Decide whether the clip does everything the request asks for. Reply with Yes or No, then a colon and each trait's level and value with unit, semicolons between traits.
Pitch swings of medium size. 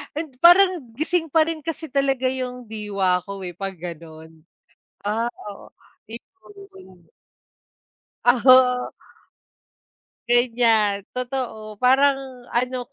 Yes: average, 4.9 semitones